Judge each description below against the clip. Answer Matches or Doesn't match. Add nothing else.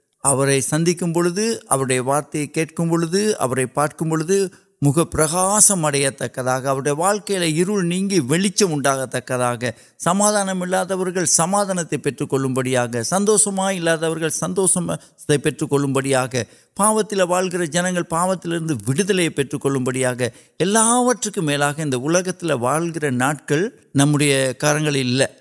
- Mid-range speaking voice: Matches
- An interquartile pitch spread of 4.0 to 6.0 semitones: Matches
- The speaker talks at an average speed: Doesn't match